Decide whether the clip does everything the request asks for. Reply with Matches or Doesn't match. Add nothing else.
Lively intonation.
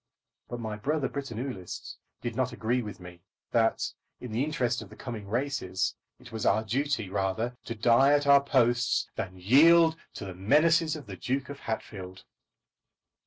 Doesn't match